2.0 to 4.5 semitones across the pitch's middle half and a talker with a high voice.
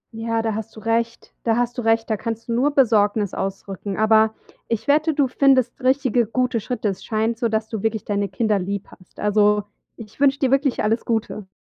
Yes: narrow, 2.5 semitones; high, 225 Hz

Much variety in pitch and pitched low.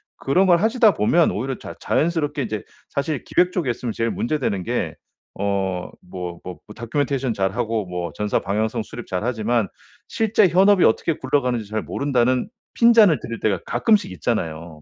Yes: wide, 7.2 semitones; low, 120 Hz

